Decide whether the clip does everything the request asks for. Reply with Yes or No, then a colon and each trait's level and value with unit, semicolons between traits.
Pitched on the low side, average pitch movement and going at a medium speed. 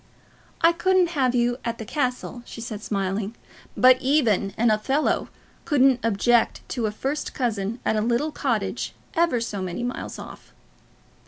No: high, 240 Hz; average, 3.9 semitones; average, 155 wpm